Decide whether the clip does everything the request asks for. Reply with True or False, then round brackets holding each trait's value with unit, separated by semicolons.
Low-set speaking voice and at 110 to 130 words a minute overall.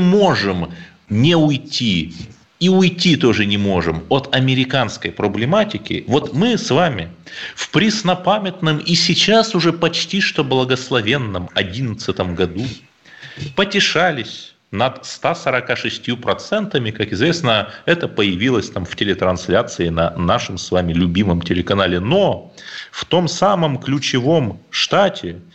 True (130 Hz; 115 wpm)